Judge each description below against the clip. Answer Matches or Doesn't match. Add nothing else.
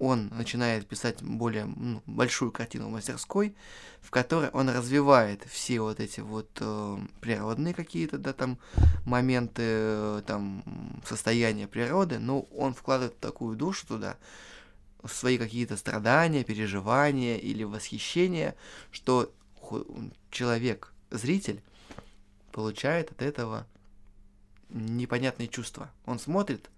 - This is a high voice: Doesn't match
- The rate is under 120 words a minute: Matches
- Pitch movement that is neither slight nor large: Matches